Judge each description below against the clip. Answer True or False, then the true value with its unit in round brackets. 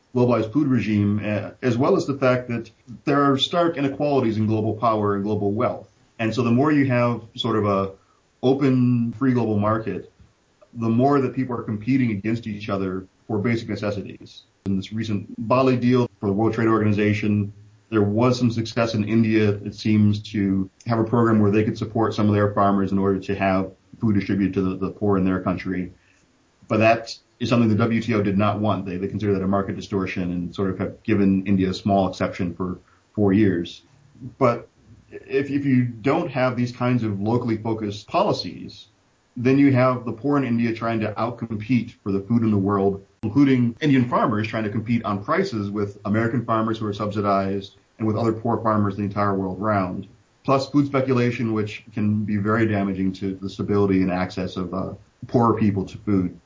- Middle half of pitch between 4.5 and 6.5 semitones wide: False (3.1 semitones)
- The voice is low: True (110 Hz)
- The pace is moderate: True (195 wpm)